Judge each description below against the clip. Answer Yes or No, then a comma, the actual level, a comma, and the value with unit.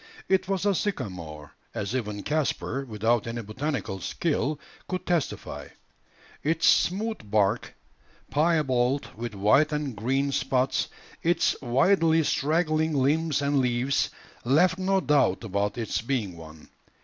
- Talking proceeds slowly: Yes, slow, 125 wpm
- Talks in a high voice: No, low, 135 Hz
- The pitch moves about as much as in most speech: No, wide, 6.3 semitones